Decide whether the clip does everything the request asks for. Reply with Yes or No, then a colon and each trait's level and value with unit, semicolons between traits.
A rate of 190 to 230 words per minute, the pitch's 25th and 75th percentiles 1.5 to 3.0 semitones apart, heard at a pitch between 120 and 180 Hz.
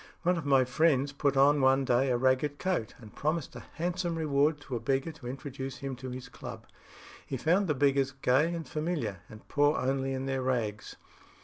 Yes: average, 200 wpm; average, 2.7 semitones; low, 135 Hz